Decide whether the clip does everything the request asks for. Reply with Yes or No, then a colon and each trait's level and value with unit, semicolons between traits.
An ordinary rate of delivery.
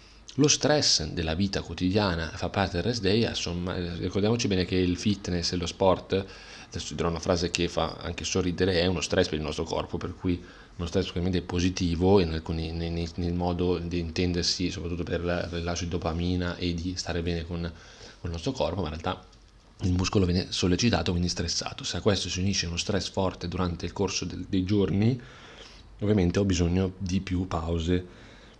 No: fast, 185 wpm